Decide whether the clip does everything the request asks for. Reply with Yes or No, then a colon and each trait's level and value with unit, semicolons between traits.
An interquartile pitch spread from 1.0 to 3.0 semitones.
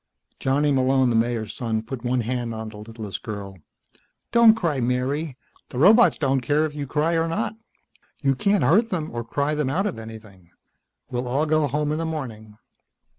No: average, 5.0 semitones